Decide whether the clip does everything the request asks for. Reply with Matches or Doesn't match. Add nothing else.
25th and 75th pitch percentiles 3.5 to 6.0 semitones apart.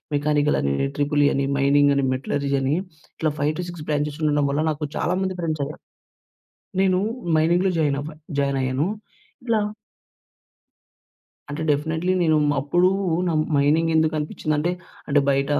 Doesn't match